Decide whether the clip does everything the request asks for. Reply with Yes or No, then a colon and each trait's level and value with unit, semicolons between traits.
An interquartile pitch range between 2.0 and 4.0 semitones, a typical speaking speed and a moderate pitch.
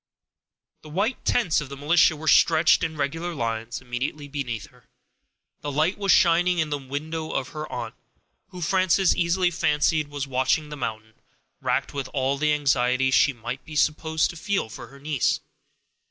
Yes: average, 3.6 semitones; average, 170 wpm; medium, 150 Hz